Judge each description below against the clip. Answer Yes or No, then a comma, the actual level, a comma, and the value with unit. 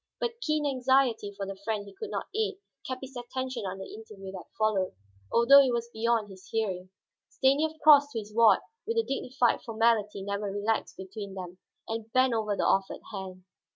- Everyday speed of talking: Yes, average, 190 wpm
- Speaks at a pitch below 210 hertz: No, high, 225 Hz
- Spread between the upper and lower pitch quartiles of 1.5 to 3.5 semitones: No, average, 4.6 semitones